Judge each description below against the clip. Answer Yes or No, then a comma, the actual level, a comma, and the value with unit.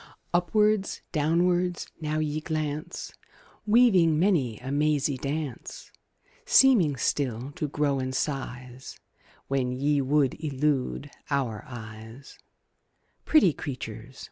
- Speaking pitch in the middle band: Yes, medium, 145 Hz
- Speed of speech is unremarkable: No, slow, 100 wpm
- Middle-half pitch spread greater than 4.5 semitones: No, average, 3.6 semitones